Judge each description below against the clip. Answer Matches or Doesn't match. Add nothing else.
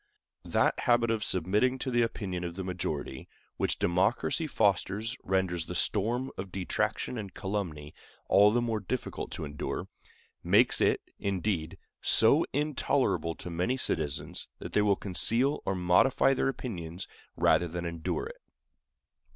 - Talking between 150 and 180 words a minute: Doesn't match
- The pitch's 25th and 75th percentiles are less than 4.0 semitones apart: Doesn't match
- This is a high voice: Doesn't match